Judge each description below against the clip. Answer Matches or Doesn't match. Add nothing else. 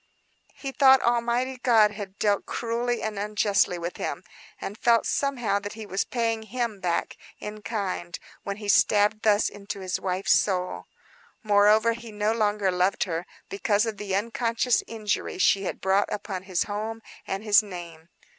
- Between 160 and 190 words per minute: Matches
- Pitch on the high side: Matches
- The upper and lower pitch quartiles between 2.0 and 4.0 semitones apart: Matches